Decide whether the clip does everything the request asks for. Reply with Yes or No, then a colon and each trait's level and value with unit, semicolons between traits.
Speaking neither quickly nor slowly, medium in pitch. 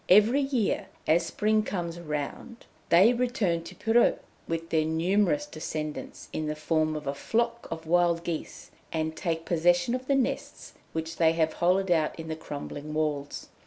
Yes: average, 165 wpm; medium, 170 Hz